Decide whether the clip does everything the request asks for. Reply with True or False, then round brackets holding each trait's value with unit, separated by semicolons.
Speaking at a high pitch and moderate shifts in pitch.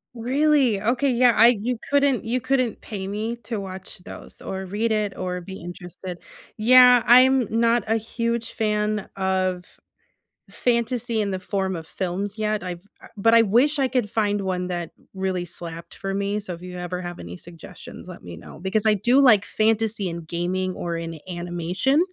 True (205 Hz; 4.4 semitones)